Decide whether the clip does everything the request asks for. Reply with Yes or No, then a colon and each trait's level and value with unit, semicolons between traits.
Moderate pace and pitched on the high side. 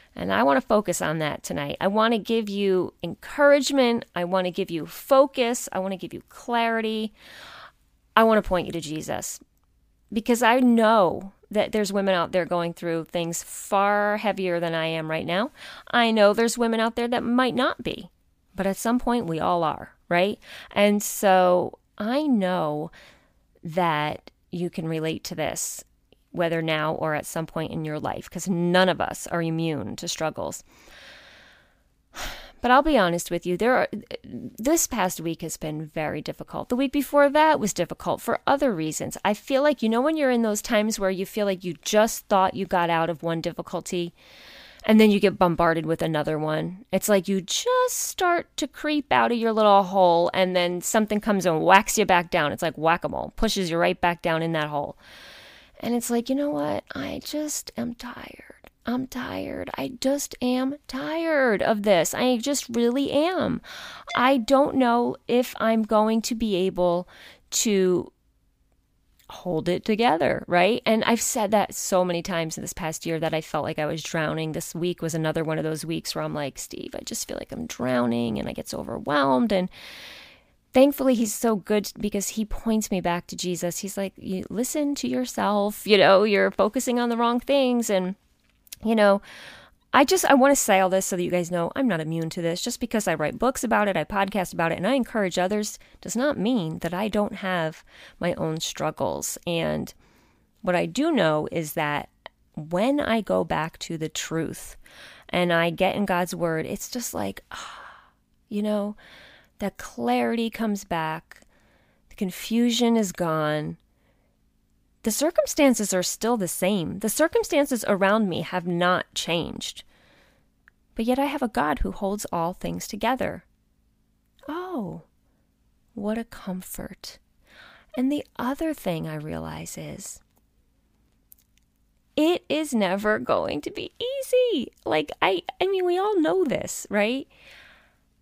Yes: average, 180 wpm; high, 205 Hz